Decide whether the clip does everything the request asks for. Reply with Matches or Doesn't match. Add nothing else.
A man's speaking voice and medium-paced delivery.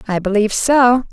Doesn't match